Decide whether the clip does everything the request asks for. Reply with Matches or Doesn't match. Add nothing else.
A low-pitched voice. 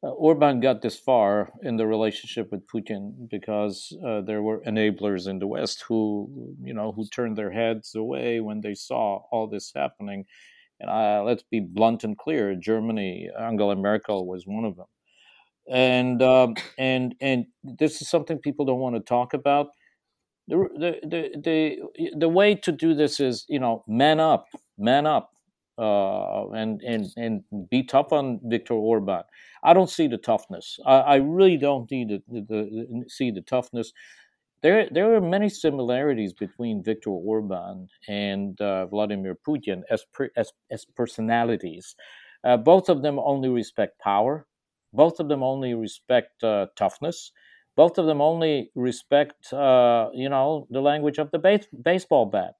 Matches